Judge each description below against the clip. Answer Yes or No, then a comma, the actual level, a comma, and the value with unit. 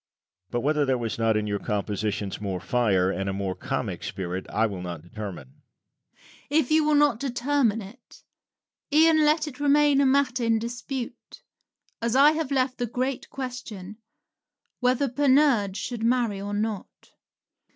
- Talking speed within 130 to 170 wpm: Yes, average, 160 wpm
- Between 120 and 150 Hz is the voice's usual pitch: No, high, 230 Hz